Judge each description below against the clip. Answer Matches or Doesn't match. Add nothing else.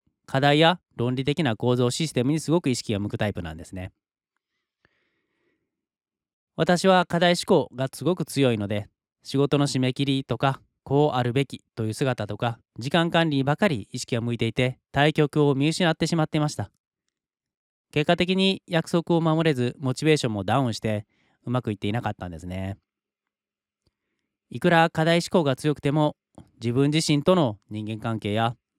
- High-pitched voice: Doesn't match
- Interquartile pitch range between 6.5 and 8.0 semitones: Doesn't match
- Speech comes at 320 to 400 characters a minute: Matches